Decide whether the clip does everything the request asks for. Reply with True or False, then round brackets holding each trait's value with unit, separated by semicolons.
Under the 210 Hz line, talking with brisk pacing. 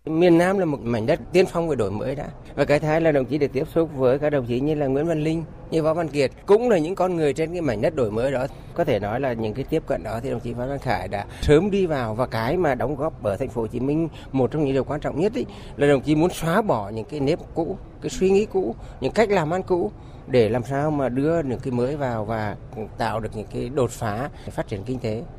True (140 Hz; 295 wpm)